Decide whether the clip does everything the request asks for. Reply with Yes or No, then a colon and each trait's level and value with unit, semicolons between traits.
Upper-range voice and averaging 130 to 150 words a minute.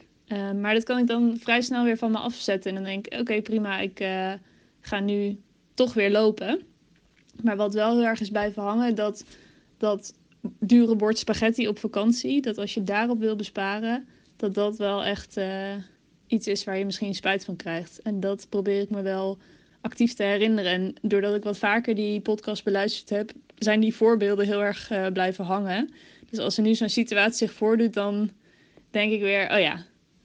No: high, 210 Hz; fast, 200 wpm